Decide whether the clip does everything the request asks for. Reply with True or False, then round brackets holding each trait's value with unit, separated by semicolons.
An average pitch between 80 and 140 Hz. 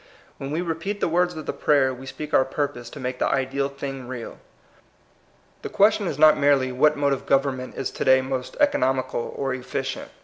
True (135 Hz)